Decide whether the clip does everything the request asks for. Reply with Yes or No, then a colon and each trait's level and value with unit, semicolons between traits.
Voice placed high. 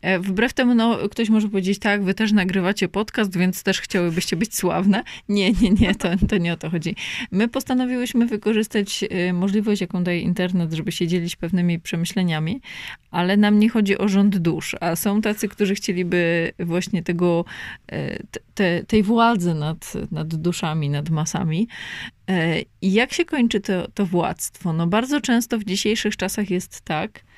Yes: high, 195 Hz